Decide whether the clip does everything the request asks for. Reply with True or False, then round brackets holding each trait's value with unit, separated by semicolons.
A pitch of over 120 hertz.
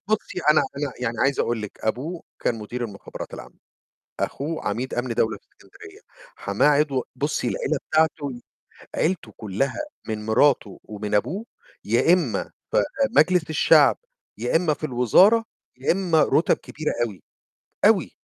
True (140 Hz)